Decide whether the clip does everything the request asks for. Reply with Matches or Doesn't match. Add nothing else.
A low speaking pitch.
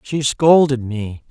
Matches